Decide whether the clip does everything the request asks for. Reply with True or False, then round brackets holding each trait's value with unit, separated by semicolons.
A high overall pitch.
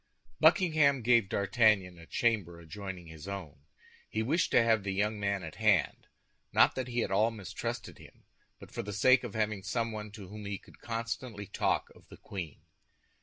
False (105 Hz)